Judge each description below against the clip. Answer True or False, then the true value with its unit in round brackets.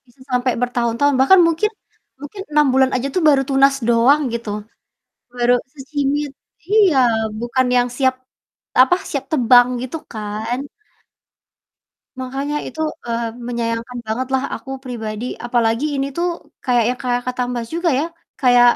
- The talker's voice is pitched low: False (255 Hz)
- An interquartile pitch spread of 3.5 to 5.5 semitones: False (2.8 semitones)